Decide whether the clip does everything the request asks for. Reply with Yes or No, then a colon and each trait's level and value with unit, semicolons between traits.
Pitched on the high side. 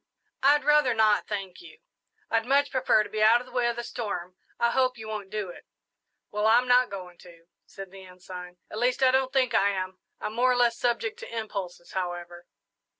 Yes: high, 220 Hz